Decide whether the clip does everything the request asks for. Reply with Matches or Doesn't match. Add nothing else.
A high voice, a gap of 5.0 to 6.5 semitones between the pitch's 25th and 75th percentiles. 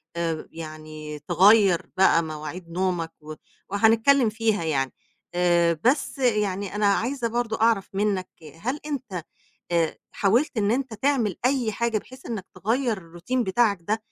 Matches